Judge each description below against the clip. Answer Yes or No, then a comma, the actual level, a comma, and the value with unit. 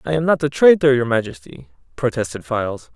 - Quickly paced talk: No, average, 185 wpm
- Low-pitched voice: Yes, low, 125 Hz